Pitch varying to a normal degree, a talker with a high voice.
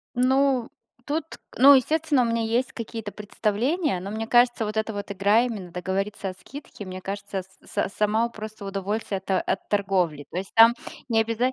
Yes: average, 3.5 semitones; high, 220 Hz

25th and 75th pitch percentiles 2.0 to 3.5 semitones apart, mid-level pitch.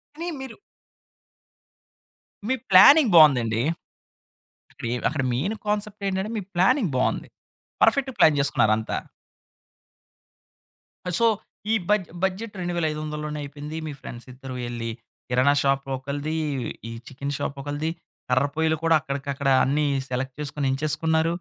No: average, 5.1 semitones; medium, 150 Hz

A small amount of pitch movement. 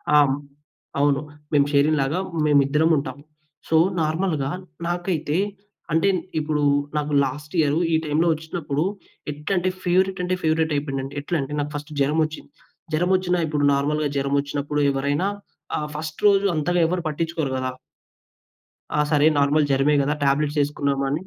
Yes: narrow, 2.3 semitones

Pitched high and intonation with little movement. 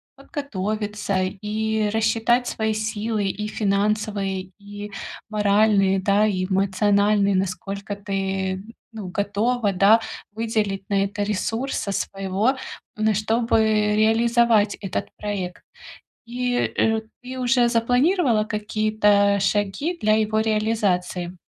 Yes: high, 210 Hz; narrow, 2.0 semitones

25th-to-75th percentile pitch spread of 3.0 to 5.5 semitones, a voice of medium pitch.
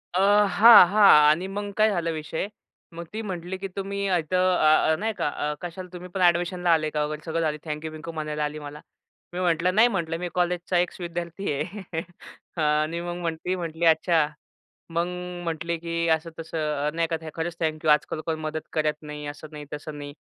No: narrow, 2.5 semitones; medium, 165 Hz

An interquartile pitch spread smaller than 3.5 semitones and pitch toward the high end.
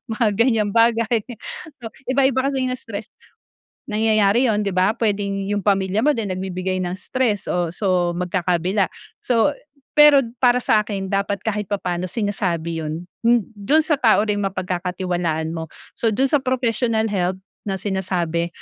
No: average, 3.9 semitones; high, 205 Hz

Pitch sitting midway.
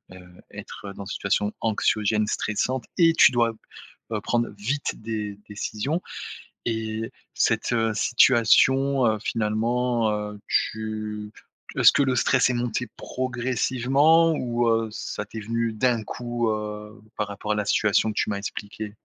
No: low, 110 Hz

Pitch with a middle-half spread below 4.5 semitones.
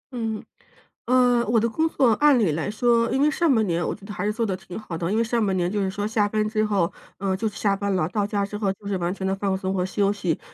Yes: average, 3.0 semitones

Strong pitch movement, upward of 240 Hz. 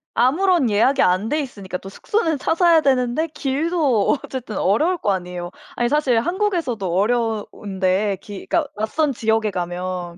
No: wide, 7.7 semitones; high, 235 Hz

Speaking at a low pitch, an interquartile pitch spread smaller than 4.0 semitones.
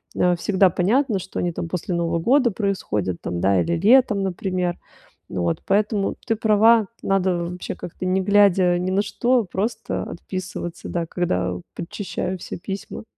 No: medium, 185 Hz; average, 2.9 semitones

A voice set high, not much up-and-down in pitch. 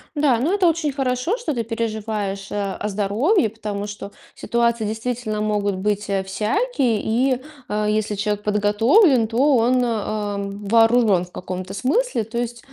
No: high, 220 Hz; average, 3.2 semitones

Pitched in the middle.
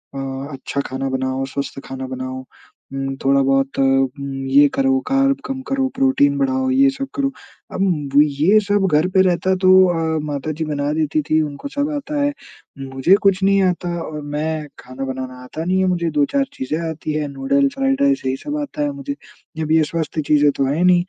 Yes: medium, 155 Hz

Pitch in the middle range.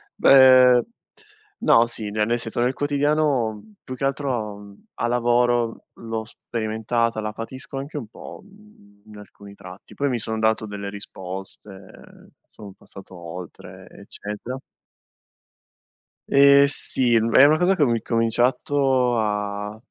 No: low, 115 Hz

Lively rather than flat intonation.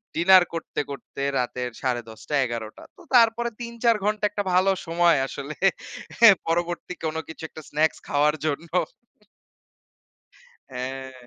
Yes: wide, 5.9 semitones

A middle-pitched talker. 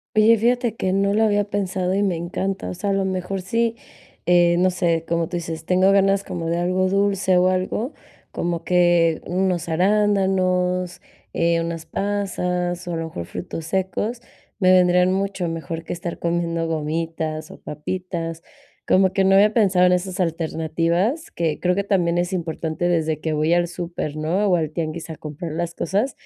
Yes: medium, 180 Hz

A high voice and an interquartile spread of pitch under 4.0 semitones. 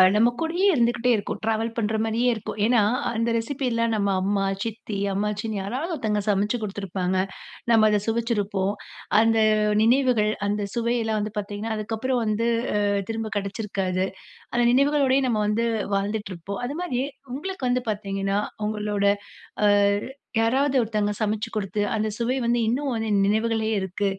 Yes: high, 220 Hz; narrow, 2.5 semitones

